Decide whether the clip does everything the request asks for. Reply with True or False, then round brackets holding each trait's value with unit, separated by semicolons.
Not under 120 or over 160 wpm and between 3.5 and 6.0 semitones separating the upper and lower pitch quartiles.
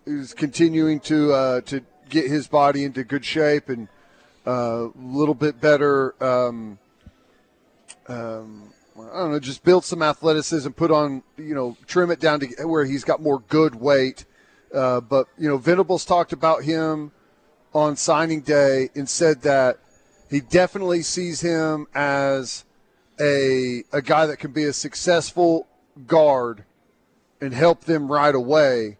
False (150 wpm; 3.1 semitones)